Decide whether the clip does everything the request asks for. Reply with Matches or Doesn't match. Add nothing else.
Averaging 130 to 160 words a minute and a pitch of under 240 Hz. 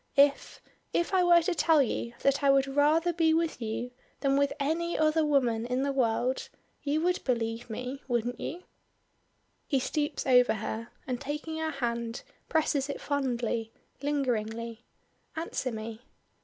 Doesn't match